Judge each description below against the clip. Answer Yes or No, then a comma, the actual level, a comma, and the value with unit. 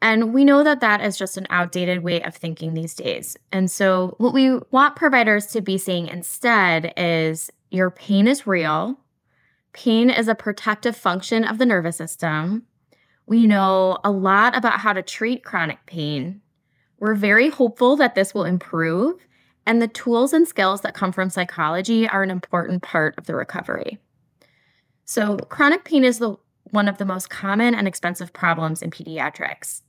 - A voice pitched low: No, high, 200 Hz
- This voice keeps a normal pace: Yes, average, 175 wpm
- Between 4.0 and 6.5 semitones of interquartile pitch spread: Yes, average, 4.6 semitones